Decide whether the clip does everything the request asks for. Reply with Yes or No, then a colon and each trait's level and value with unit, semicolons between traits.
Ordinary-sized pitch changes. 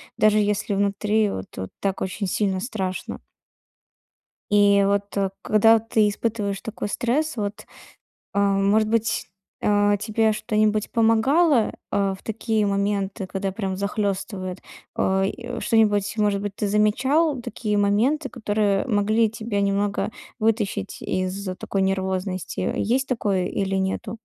No: narrow, 2.0 semitones